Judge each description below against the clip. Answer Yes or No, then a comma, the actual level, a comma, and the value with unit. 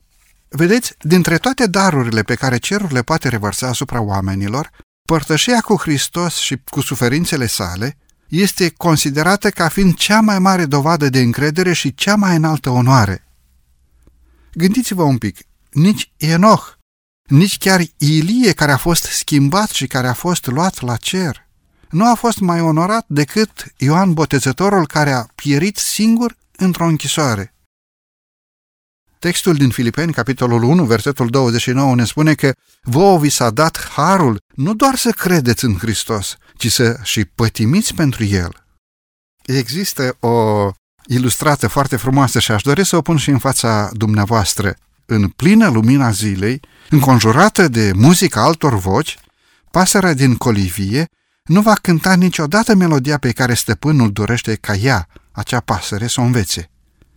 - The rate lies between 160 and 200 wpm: No, average, 145 wpm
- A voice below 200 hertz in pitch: Yes, medium, 140 Hz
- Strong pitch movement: Yes, wide, 7.1 semitones